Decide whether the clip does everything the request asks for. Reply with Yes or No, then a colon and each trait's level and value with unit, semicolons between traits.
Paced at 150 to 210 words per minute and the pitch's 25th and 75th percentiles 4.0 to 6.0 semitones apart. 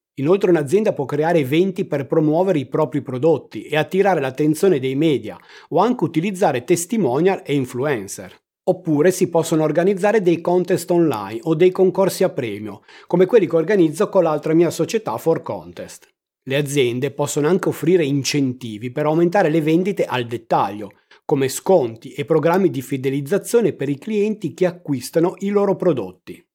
Yes: average, 155 wpm; average, 4.5 semitones